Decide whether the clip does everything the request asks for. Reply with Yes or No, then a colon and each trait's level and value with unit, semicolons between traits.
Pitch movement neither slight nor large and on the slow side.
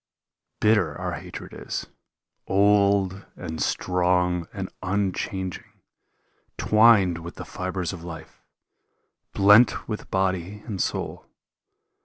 No: narrow, 2.2 semitones; slow, 100 wpm